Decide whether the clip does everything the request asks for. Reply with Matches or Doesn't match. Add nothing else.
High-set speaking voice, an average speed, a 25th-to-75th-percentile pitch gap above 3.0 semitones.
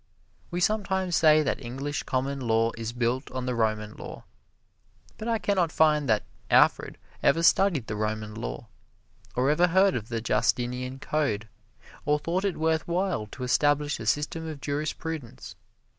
Doesn't match